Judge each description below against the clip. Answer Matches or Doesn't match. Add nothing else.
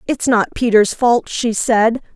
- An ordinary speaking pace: Matches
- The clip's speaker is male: Doesn't match